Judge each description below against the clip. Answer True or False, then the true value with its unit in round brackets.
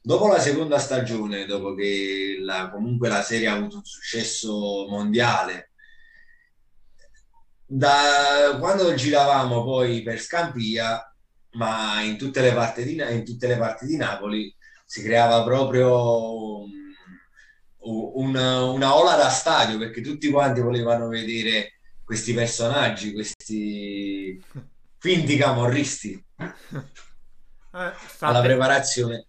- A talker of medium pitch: False (115 Hz)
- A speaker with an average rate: False (110 wpm)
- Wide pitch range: False (4.3 semitones)